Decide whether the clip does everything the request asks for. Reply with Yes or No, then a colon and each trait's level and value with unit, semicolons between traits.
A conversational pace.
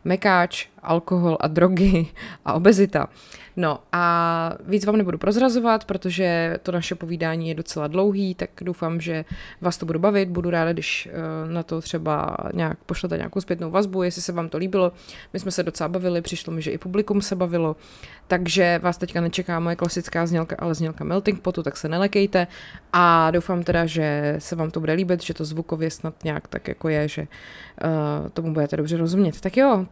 No: fast, 185 wpm